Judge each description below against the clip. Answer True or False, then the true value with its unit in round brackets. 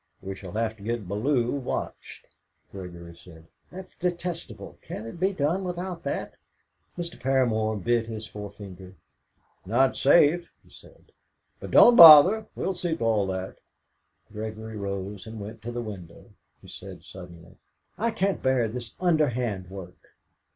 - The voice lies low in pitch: True (115 Hz)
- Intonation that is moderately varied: False (8.0 semitones)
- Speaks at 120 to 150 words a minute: True (145 wpm)